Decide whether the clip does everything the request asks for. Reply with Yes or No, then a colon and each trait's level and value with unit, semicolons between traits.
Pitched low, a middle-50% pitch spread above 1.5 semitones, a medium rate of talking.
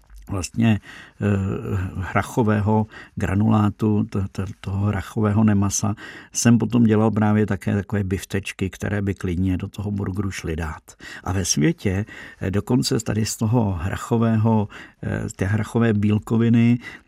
Yes: low, 105 Hz; narrow, 2.1 semitones; average, 135 wpm